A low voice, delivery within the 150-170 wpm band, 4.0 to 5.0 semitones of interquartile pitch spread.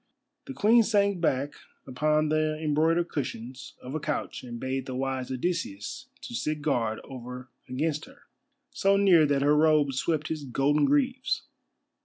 No: medium, 150 Hz; average, 155 wpm; average, 4.3 semitones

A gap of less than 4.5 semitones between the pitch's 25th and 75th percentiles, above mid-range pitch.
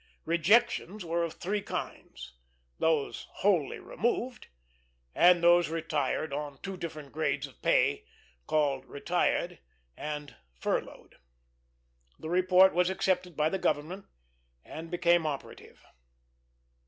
No: average, 3.2 semitones; medium, 170 Hz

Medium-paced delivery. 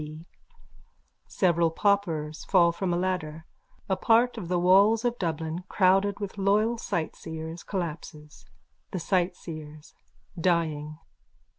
No: slow, 115 wpm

